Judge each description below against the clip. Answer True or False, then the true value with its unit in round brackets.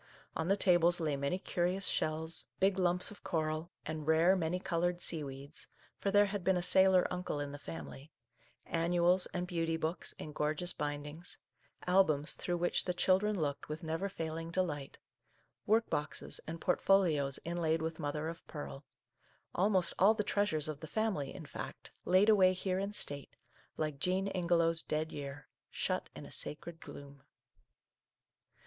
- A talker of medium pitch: True (170 Hz)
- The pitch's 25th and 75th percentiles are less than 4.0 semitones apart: True (3.3 semitones)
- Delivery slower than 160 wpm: False (165 wpm)